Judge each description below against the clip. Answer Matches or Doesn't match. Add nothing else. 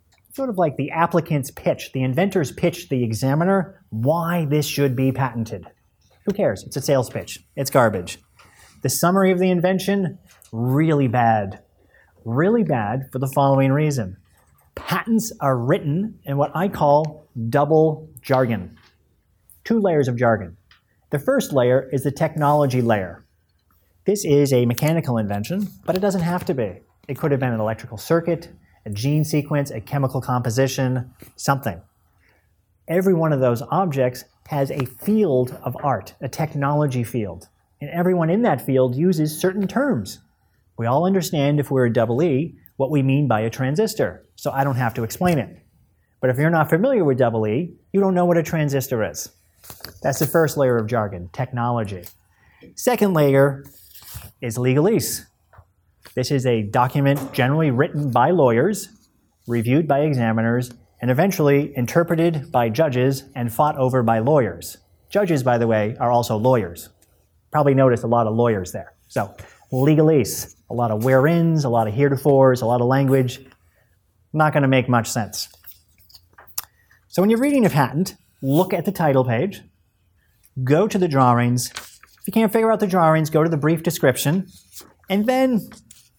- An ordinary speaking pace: Matches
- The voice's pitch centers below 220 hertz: Matches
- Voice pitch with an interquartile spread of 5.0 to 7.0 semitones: Matches